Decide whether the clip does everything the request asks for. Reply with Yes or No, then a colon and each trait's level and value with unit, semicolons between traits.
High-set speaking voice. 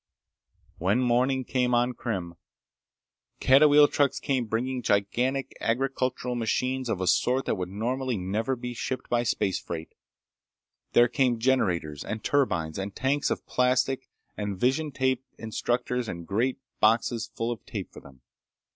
No: low, 120 Hz